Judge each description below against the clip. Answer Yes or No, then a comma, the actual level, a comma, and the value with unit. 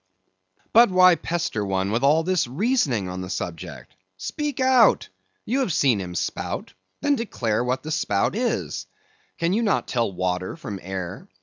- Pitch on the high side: No, low, 135 Hz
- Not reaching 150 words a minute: No, average, 165 wpm